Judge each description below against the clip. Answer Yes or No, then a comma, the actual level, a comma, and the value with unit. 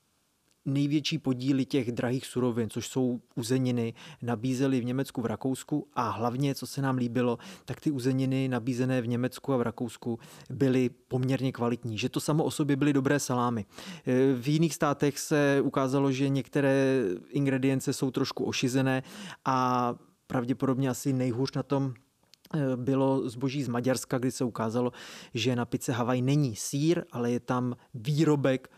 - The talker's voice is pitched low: Yes, low, 130 Hz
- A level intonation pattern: Yes, narrow, 2.0 semitones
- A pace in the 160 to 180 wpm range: No, average, 150 wpm